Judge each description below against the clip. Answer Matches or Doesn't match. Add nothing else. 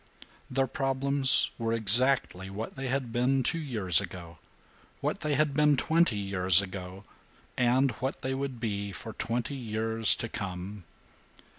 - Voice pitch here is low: Matches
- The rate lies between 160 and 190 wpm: Doesn't match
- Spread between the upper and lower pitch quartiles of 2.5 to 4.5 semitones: Doesn't match